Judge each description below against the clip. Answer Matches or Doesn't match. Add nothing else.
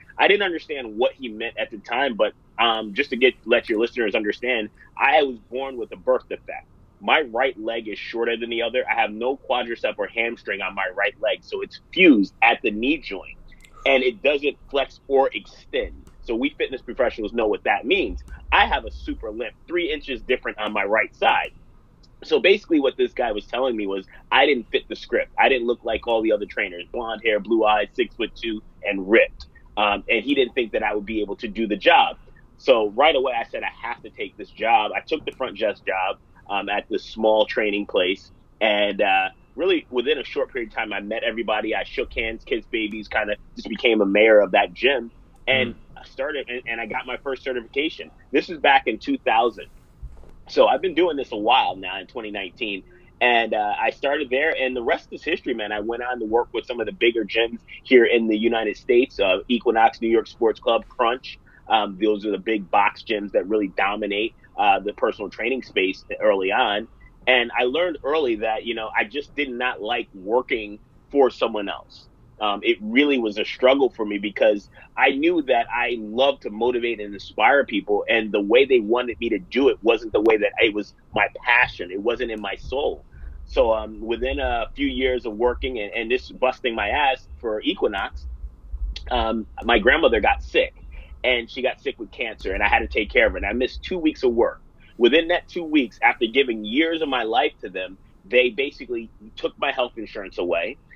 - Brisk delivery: Matches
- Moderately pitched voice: Doesn't match